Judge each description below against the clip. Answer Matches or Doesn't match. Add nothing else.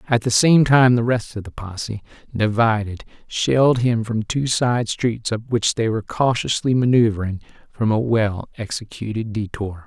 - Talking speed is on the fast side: Doesn't match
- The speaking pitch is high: Doesn't match